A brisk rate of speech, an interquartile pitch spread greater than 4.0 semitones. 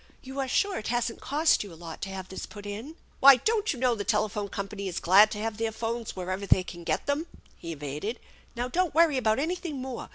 Yes: fast, 260 wpm; wide, 5.5 semitones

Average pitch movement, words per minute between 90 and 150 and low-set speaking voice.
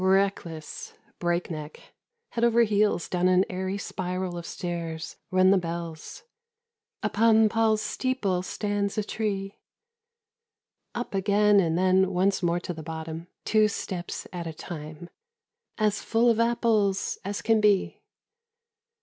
No: average, 3.7 semitones; average, 140 wpm; high, 195 Hz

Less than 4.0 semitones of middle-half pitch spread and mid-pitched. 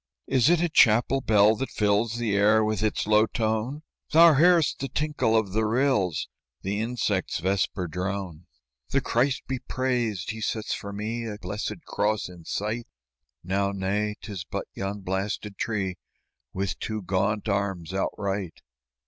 No: average, 3.1 semitones; low, 105 Hz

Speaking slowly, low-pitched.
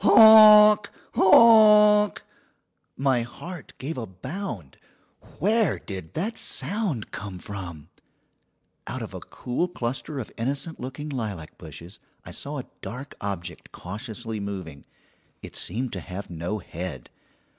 Yes: slow, 125 wpm; low, 125 Hz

